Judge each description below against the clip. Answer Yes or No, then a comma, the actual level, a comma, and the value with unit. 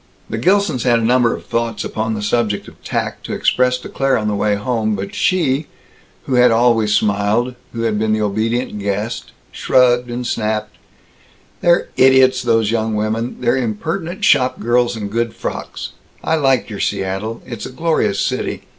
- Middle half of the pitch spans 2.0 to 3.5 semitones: Yes, average, 2.9 semitones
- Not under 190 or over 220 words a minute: No, average, 175 wpm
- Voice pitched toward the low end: Yes, low, 115 Hz